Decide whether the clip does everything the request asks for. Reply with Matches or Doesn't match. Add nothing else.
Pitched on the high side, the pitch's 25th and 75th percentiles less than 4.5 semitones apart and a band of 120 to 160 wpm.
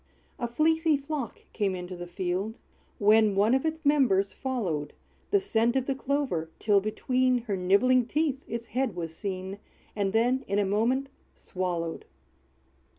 Doesn't match